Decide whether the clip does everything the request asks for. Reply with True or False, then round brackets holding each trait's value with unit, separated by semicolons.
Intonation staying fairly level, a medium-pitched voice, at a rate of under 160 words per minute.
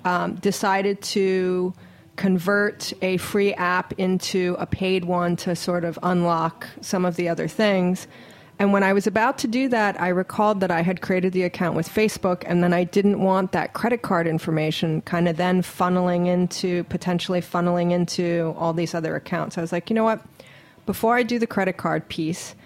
False (2.2 semitones; 180 Hz; 190 wpm)